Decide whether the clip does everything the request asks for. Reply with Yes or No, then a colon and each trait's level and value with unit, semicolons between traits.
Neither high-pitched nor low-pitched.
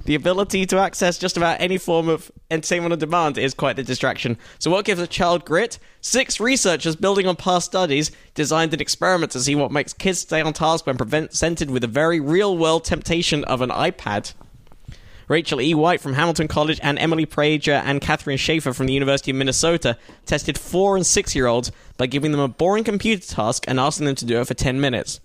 Yes: medium, 155 Hz